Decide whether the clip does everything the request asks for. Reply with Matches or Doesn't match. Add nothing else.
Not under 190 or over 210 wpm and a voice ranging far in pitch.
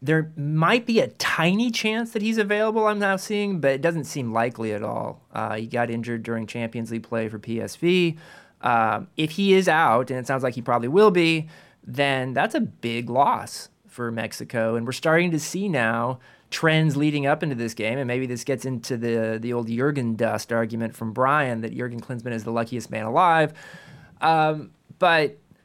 Matches